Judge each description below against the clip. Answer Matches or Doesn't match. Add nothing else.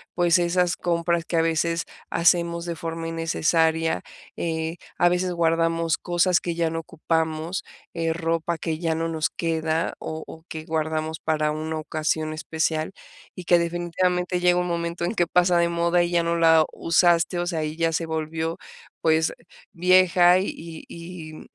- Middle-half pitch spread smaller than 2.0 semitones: Matches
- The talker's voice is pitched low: Doesn't match